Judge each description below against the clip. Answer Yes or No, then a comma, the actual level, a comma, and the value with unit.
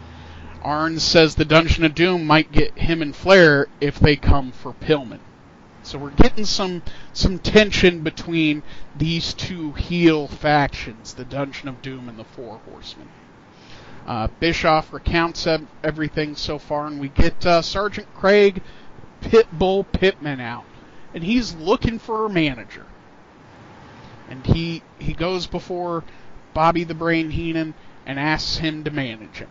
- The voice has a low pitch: No, medium, 155 Hz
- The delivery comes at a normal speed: Yes, average, 145 wpm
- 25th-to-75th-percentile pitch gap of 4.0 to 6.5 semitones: No, average, 3.3 semitones